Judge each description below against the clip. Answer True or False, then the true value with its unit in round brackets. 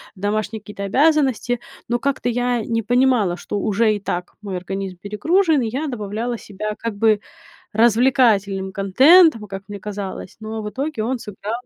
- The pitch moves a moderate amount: True (3.6 semitones)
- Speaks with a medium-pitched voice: False (220 Hz)